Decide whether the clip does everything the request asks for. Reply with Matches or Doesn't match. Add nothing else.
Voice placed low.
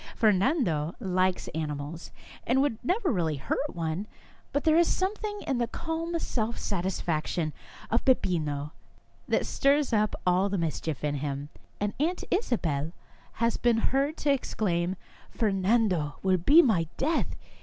Doesn't match